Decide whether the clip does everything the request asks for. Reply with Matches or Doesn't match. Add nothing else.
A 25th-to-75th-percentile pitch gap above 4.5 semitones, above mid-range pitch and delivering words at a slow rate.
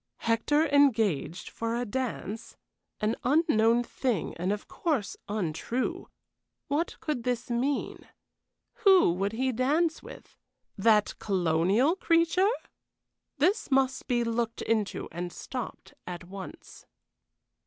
Matches